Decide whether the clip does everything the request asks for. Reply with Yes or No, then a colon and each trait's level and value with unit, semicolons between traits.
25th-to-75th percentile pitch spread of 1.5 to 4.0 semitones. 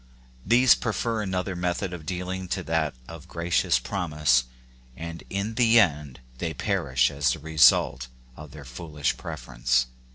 No: average, 4.9 semitones